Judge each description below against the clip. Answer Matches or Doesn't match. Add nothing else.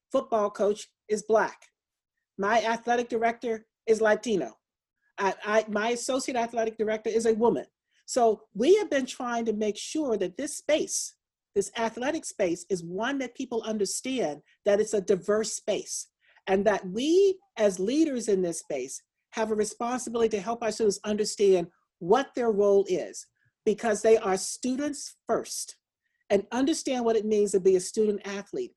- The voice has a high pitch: Matches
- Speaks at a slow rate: Doesn't match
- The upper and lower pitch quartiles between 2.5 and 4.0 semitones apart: Matches